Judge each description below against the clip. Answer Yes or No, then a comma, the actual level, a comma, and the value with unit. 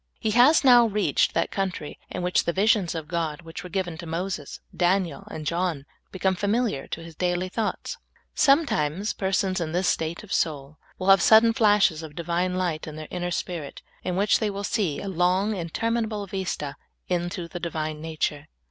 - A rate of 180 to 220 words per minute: Yes, average, 185 wpm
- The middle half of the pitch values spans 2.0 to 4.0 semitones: Yes, average, 3.6 semitones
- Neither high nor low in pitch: Yes, medium, 180 Hz